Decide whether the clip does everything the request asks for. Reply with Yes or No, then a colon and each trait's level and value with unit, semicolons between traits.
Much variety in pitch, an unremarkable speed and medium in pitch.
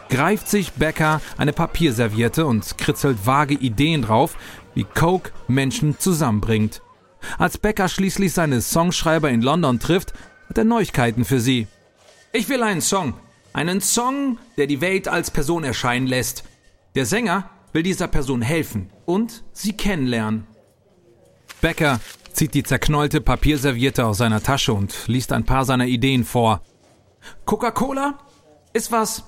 Yes: wide, 7.0 semitones; average, 135 wpm; medium, 145 Hz